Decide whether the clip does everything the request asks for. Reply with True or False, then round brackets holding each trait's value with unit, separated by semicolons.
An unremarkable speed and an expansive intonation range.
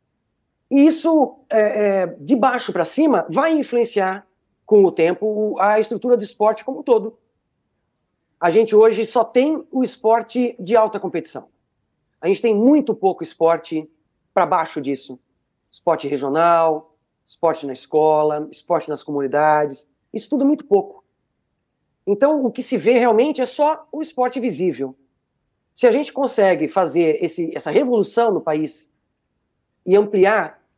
True (140 wpm; 7.4 semitones)